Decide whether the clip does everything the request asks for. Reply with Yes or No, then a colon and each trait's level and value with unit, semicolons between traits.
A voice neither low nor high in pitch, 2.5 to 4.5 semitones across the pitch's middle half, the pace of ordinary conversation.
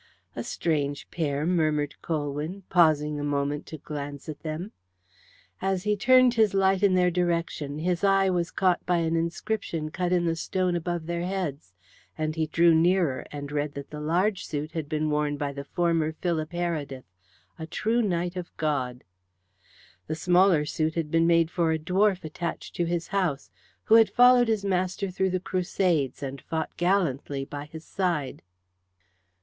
Yes: medium, 165 Hz; average, 3.4 semitones; average, 170 wpm